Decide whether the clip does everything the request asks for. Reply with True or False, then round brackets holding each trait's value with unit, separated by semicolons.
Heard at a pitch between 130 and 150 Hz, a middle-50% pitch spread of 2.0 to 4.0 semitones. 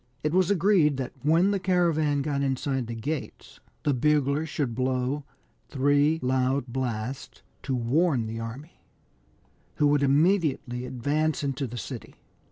True (140 Hz; 3.3 semitones)